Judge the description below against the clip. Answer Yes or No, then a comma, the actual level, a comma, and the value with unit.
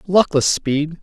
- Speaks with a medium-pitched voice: Yes, medium, 155 Hz